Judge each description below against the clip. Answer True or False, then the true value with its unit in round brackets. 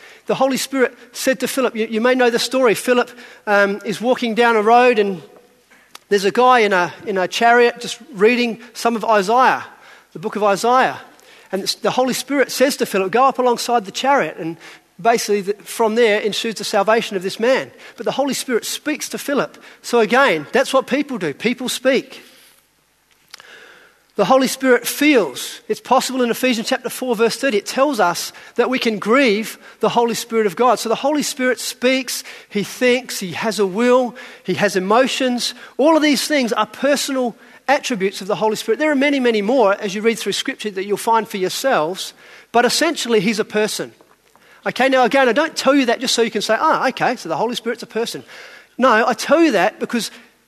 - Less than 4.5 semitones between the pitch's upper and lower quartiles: True (3.1 semitones)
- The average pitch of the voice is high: True (235 Hz)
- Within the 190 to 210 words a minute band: True (205 wpm)